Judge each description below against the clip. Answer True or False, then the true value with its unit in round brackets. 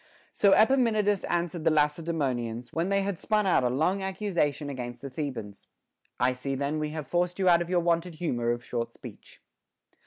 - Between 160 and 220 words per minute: True (185 wpm)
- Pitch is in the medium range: True (160 Hz)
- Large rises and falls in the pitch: True (6.0 semitones)